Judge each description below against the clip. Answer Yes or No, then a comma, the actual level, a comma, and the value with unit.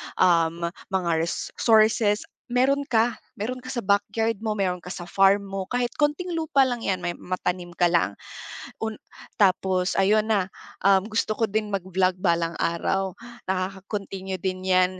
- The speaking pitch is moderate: No, high, 195 Hz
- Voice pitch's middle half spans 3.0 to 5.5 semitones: Yes, average, 3.3 semitones